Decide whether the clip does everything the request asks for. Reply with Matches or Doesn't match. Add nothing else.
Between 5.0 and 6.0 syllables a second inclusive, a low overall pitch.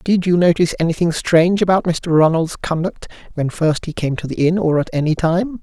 Doesn't match